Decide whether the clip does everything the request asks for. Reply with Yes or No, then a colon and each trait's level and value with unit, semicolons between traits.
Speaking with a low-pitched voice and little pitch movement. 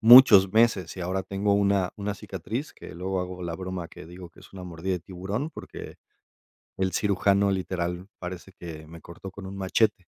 Yes: very low, 95 Hz; narrow, 2.0 semitones